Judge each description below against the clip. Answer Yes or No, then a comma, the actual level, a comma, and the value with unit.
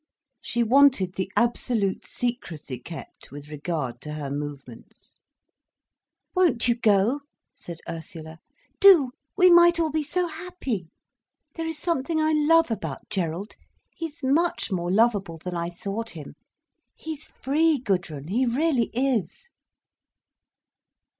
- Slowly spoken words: Yes, slow, 120 wpm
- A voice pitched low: No, high, 230 Hz